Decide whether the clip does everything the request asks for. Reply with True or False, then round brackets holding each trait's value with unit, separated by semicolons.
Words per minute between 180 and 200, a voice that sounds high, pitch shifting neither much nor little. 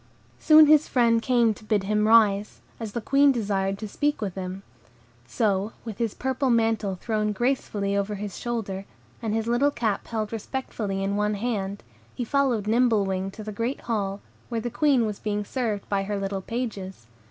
True (185 wpm; 215 Hz; 3.1 semitones)